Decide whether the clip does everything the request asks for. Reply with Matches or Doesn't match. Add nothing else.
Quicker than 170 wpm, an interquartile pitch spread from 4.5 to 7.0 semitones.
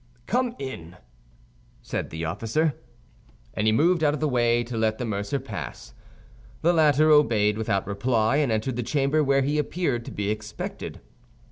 Doesn't match